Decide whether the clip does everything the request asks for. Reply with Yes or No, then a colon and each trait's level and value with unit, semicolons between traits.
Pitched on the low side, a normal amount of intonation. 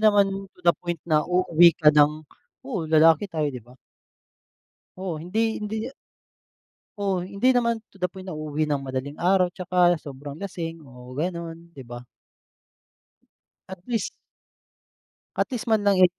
No: medium, 175 Hz; average, 4.2 semitones